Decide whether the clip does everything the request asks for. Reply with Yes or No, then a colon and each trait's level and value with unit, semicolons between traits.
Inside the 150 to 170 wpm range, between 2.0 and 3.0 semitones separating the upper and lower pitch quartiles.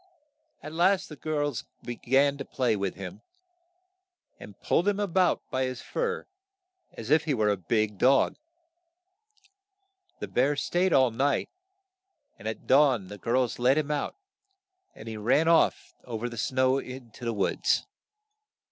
No: average, 155 wpm; average, 4.5 semitones